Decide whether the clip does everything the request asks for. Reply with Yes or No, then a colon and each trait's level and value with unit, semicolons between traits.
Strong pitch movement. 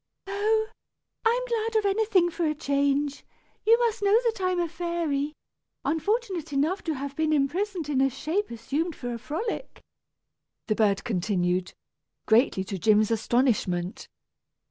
Yes: wide, 8.4 semitones